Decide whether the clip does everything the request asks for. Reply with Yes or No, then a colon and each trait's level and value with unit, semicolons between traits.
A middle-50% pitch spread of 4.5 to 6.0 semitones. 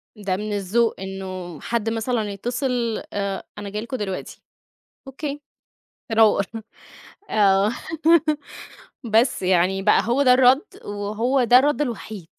No: average, 3.8 semitones